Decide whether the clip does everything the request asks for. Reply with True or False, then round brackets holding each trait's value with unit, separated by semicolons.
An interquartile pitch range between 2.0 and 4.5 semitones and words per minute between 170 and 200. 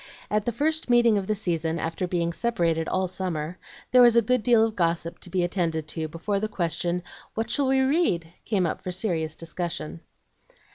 False (5.1 semitones; 195 wpm)